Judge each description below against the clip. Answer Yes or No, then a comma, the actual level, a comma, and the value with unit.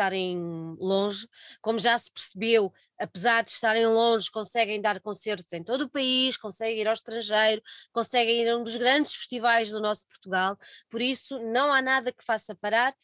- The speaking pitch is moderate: No, high, 225 Hz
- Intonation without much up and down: Yes, narrow, 2.3 semitones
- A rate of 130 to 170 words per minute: No, average, 180 wpm